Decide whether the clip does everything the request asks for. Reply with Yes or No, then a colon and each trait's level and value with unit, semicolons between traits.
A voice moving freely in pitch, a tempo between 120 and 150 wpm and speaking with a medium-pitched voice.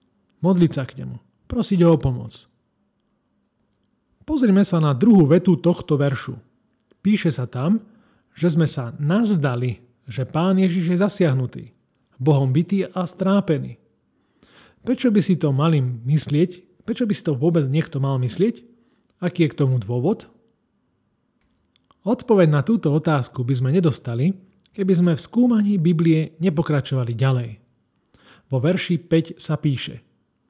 Yes: wide, 5.9 semitones; average, 135 wpm; medium, 165 Hz